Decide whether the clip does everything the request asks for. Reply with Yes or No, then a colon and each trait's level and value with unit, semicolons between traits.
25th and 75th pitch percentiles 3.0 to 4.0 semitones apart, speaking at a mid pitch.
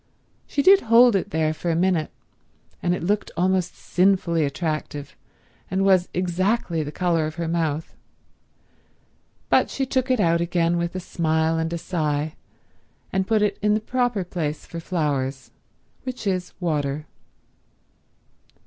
Yes: average, 3.4 semitones; medium, 175 Hz